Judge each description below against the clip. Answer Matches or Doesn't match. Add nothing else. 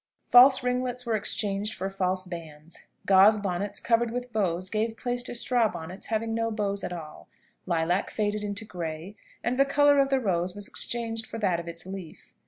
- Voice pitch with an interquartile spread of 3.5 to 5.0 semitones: Matches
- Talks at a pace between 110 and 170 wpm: Doesn't match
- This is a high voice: Matches